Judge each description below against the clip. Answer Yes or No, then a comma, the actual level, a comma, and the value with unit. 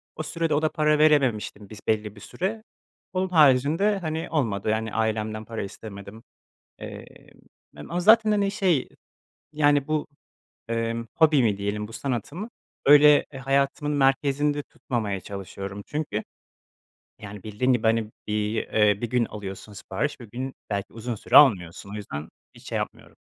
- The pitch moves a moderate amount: No, wide, 6.0 semitones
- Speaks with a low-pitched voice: Yes, low, 120 Hz